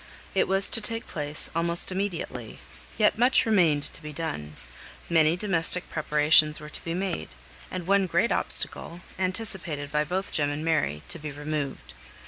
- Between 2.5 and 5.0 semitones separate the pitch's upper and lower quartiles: Yes, average, 4.1 semitones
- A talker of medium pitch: Yes, medium, 165 Hz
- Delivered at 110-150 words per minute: No, average, 160 wpm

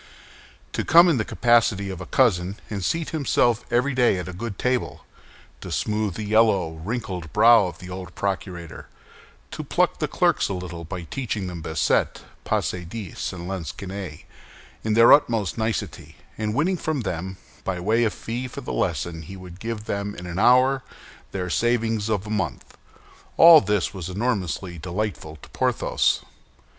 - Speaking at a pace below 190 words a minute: Yes, average, 165 wpm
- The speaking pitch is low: Yes, low, 100 Hz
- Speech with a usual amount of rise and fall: Yes, average, 4.4 semitones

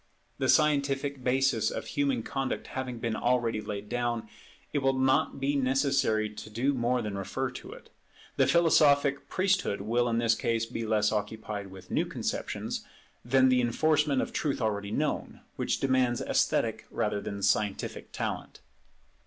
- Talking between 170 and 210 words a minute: No, average, 160 wpm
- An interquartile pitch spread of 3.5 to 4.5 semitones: Yes, average, 3.9 semitones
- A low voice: Yes, low, 125 Hz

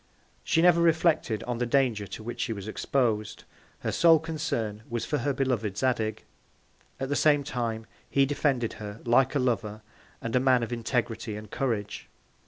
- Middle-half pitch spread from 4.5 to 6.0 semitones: No, average, 3.9 semitones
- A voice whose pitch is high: No, low, 120 Hz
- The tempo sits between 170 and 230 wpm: Yes, average, 175 wpm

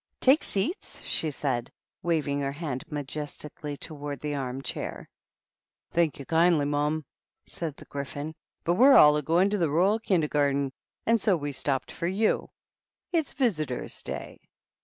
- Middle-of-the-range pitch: Yes, medium, 150 Hz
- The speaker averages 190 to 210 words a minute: No, average, 165 wpm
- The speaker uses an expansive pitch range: No, average, 3.6 semitones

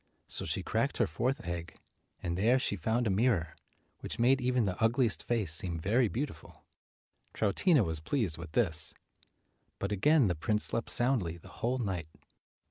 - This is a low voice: Yes, low, 105 Hz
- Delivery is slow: No, average, 165 wpm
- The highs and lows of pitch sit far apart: Yes, wide, 6.3 semitones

